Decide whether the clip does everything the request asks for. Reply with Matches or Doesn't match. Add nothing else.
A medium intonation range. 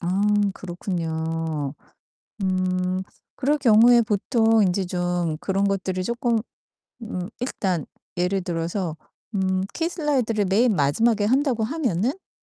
Matches